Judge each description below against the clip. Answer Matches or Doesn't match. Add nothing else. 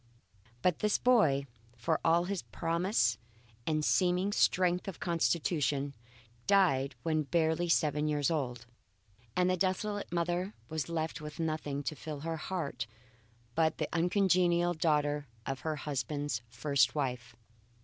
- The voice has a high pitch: Doesn't match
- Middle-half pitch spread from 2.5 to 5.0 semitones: Matches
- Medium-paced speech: Doesn't match